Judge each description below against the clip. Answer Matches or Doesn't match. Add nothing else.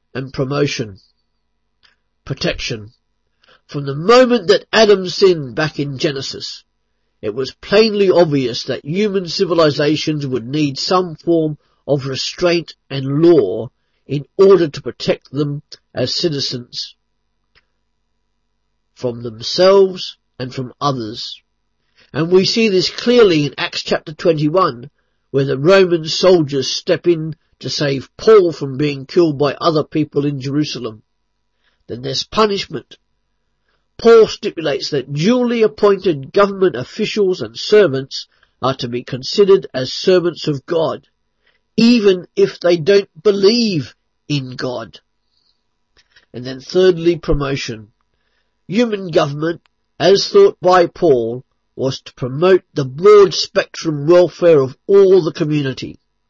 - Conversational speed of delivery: Doesn't match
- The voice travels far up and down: Matches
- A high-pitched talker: Doesn't match